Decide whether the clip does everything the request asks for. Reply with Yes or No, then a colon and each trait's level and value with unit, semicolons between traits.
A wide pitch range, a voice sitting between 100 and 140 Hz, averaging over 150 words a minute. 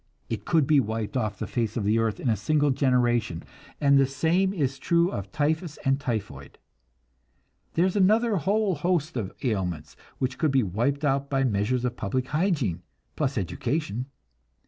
Yes: wide, 5.7 semitones; low, 135 Hz; average, 170 wpm